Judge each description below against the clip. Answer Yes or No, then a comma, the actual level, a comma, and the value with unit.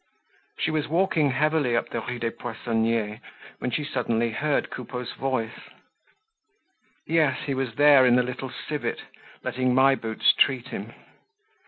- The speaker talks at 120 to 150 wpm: Yes, average, 145 wpm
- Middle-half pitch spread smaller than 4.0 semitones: Yes, average, 3.6 semitones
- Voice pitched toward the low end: Yes, low, 130 Hz